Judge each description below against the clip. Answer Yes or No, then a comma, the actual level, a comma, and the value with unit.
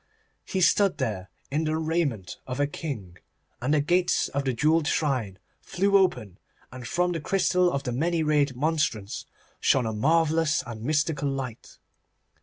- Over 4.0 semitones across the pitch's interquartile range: Yes, average, 4.8 semitones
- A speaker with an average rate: Yes, average, 160 wpm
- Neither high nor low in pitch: Yes, medium, 145 Hz